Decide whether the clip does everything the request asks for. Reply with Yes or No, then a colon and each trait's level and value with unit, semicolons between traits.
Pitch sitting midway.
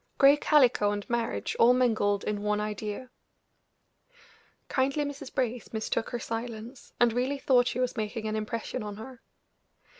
No: high, 235 Hz